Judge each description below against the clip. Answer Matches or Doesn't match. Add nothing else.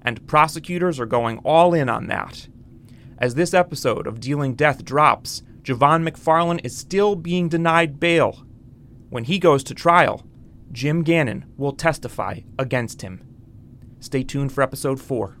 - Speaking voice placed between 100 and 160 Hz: Matches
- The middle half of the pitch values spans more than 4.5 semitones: Matches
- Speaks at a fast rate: Doesn't match